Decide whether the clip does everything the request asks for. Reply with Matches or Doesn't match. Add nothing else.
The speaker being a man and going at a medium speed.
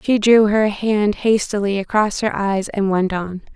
Doesn't match